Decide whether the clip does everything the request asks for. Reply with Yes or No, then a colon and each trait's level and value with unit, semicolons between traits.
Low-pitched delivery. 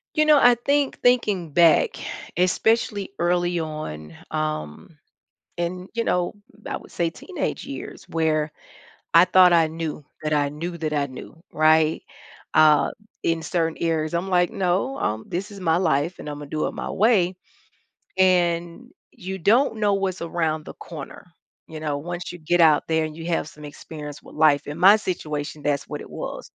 No: medium, 165 Hz